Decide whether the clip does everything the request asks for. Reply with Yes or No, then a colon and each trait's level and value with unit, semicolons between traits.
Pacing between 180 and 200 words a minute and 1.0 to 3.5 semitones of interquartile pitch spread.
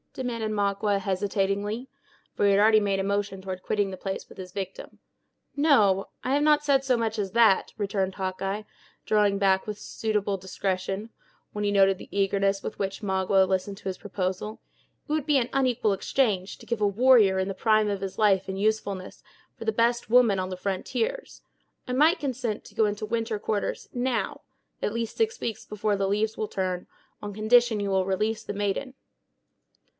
Yes: average, 190 wpm; average, 2.9 semitones